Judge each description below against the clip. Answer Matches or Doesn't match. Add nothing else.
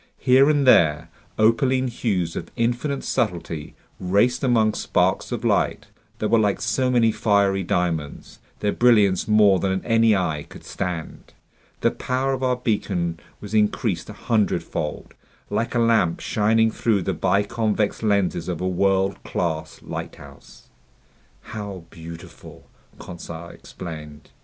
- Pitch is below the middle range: Matches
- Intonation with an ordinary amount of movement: Matches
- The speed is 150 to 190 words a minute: Doesn't match